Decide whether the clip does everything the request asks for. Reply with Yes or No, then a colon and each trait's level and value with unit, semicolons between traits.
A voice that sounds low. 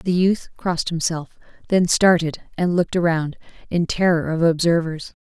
No: medium, 170 Hz